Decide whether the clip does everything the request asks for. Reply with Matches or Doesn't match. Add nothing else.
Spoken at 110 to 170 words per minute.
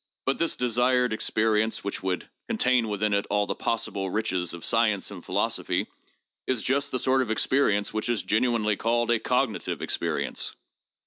Matches